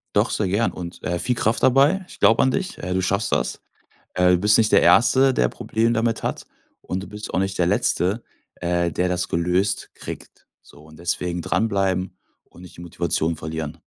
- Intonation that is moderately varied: Yes, average, 4.2 semitones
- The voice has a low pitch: Yes, very low, 95 Hz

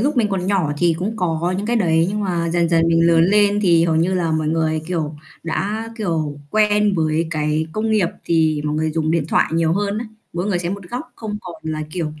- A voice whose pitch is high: No, medium, 170 Hz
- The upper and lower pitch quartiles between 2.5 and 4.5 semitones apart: Yes, average, 4.1 semitones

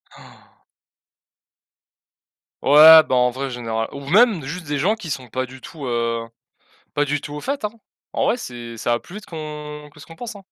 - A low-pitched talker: No, medium, 145 Hz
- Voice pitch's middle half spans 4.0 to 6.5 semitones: Yes, average, 5.1 semitones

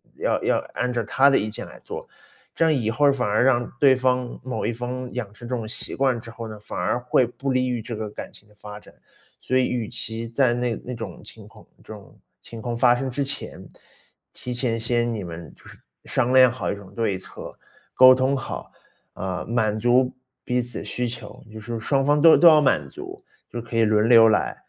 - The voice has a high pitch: No, low, 120 Hz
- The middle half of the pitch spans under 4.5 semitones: Yes, narrow, 2.6 semitones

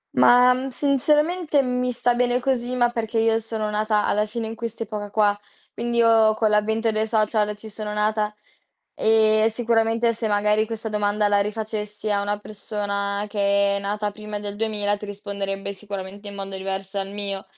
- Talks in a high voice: Yes, high, 215 Hz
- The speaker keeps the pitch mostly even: Yes, narrow, 1.9 semitones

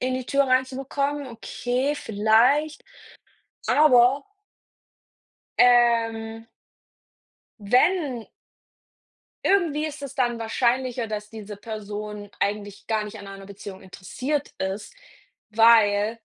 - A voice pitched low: No, high, 235 Hz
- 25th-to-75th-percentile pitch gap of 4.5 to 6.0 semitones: No, average, 4.0 semitones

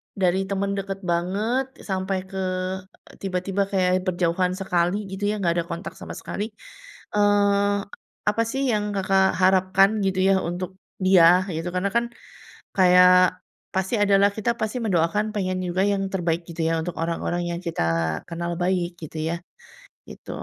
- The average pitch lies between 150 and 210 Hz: Yes, high, 190 Hz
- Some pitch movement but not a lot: No, narrow, 2.3 semitones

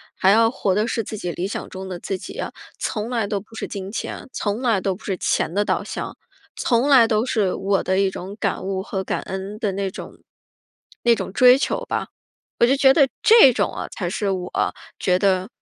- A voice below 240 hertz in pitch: Yes, high, 200 Hz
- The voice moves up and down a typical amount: Yes, average, 3.3 semitones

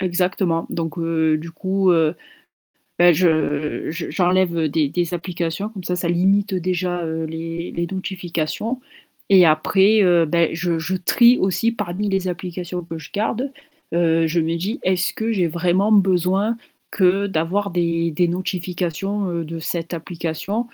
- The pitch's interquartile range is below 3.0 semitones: Yes, narrow, 2.5 semitones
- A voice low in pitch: No, medium, 175 Hz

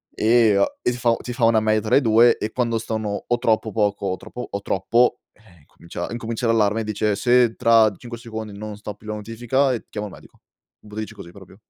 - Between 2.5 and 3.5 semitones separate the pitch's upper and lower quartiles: No, narrow, 2.0 semitones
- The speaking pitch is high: No, low, 110 Hz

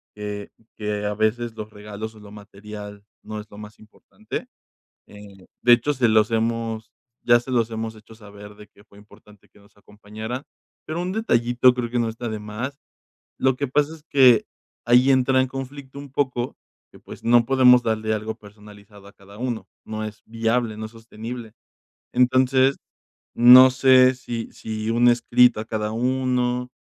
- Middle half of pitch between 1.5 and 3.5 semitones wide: Yes, average, 2.9 semitones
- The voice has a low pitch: Yes, low, 115 Hz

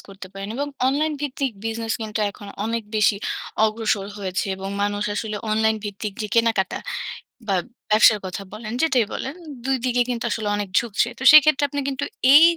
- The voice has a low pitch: No, high, 220 Hz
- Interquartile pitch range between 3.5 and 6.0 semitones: Yes, average, 4.2 semitones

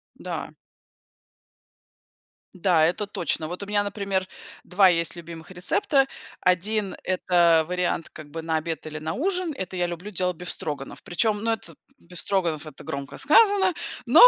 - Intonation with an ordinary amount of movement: Yes, average, 3.8 semitones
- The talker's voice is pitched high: No, medium, 180 Hz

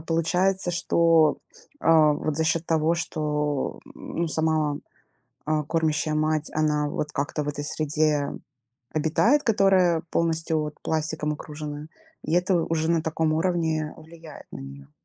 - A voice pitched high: No, medium, 155 Hz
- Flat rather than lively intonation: Yes, narrow, 1.6 semitones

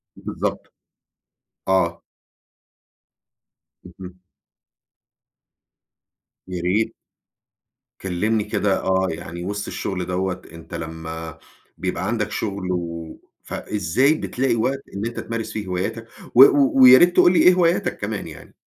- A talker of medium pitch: No, very low, 95 Hz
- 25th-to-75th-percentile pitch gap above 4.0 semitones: Yes, average, 4.6 semitones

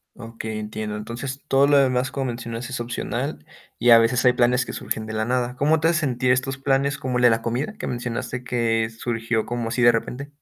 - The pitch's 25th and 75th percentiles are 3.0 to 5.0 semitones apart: No, narrow, 2.6 semitones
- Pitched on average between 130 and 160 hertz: No, low, 120 Hz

